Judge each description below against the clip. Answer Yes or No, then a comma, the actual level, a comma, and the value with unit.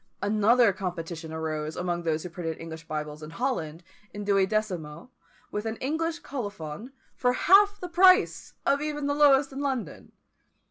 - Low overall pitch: No, high, 205 Hz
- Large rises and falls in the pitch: Yes, wide, 8.9 semitones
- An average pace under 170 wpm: Yes, average, 150 wpm